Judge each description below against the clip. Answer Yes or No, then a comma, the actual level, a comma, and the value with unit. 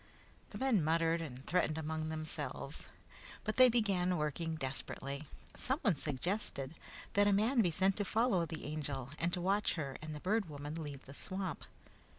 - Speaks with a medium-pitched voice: Yes, medium, 165 Hz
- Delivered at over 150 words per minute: Yes, average, 165 wpm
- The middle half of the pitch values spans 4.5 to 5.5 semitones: Yes, average, 4.8 semitones